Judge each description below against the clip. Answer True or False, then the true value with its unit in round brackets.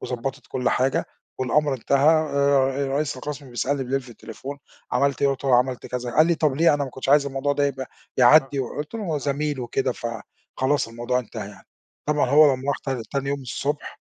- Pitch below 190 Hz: True (135 Hz)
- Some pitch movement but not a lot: False (2.3 semitones)